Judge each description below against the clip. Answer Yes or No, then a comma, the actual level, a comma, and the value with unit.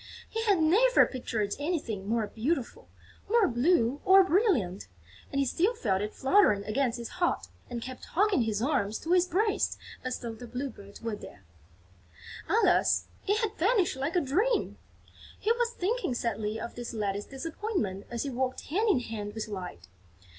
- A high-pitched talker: Yes, very high, 265 Hz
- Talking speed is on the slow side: No, average, 170 wpm